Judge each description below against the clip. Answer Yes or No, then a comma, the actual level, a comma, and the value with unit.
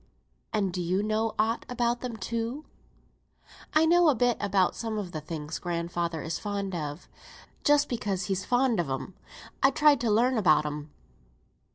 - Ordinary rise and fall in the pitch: No, wide, 5.7 semitones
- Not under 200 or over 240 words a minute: No, average, 170 wpm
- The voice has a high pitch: Yes, high, 210 Hz